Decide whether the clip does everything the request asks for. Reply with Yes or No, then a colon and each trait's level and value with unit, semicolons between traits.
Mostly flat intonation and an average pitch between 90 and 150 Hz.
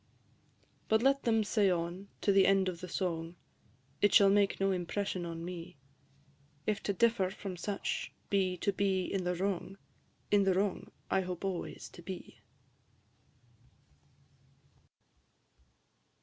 No: narrow, 2.0 semitones; high, 190 Hz